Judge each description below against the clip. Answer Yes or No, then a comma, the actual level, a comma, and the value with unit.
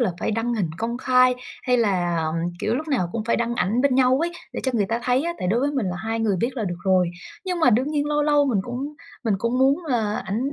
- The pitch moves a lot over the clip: No, average, 4.0 semitones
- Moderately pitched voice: No, high, 240 Hz